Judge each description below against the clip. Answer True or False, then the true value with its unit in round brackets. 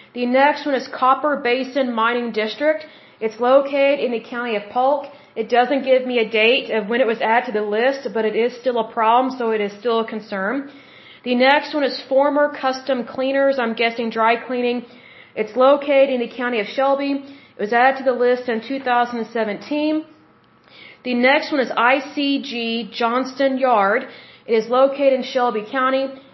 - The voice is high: True (255 Hz)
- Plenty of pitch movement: False (2.6 semitones)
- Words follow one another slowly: False (180 wpm)